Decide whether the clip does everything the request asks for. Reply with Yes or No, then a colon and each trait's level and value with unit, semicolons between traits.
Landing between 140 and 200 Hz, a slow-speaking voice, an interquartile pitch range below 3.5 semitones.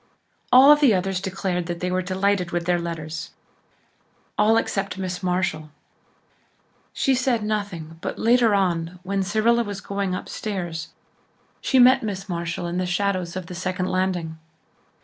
No: medium, 185 Hz; average, 150 wpm; average, 2.7 semitones